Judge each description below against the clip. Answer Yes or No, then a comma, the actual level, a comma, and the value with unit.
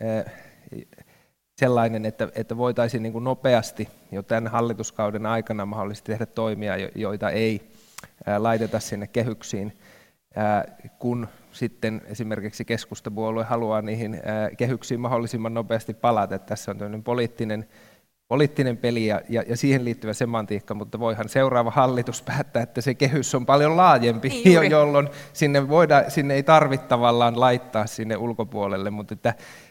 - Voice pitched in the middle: No, low, 115 Hz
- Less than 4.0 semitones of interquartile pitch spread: Yes, narrow, 2.5 semitones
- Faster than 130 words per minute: No, average, 125 wpm